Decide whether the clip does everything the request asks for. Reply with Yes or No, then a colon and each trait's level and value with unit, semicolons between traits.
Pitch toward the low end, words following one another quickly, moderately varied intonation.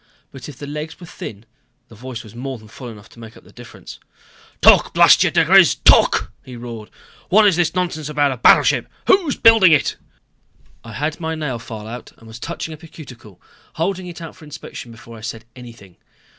No: low, 130 Hz; fast, 210 wpm; wide, 5.8 semitones